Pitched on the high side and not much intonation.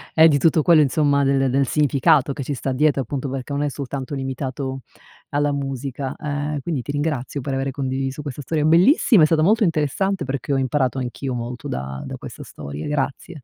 No: medium, 140 Hz; narrow, 2.2 semitones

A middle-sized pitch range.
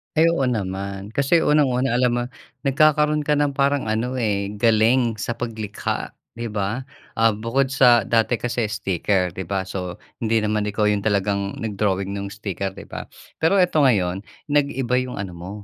Yes: average, 4.7 semitones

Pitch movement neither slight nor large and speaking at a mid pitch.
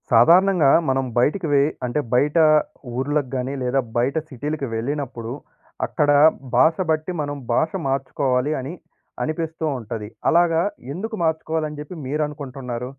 Yes: average, 3.7 semitones; medium, 145 Hz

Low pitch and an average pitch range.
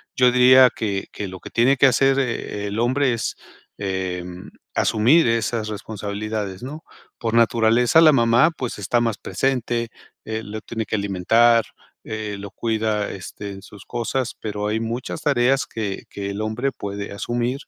Yes: low, 110 Hz; average, 3.0 semitones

